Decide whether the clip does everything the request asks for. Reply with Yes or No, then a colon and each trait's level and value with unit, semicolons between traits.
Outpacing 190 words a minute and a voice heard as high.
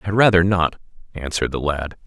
No: fast, 205 wpm; very low, 85 Hz